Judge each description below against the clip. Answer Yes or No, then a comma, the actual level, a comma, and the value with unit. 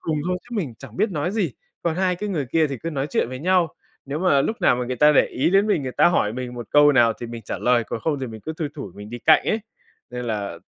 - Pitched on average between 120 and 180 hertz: Yes, medium, 140 Hz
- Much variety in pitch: Yes, wide, 6.0 semitones